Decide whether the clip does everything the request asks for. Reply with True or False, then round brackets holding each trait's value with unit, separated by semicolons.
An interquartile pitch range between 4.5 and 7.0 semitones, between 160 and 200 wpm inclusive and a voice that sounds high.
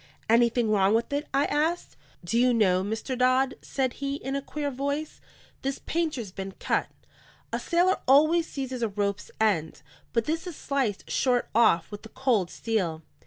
True (4.9 semitones; 170 wpm; 250 Hz)